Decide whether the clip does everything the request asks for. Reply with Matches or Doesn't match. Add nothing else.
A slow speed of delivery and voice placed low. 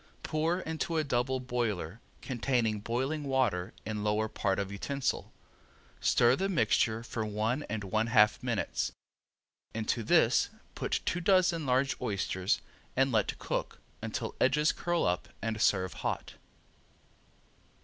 Matches